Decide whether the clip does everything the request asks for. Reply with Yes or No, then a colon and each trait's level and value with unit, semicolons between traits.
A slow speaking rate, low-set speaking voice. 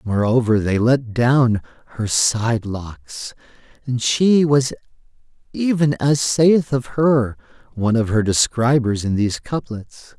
Yes: slow, 130 wpm; low, 120 Hz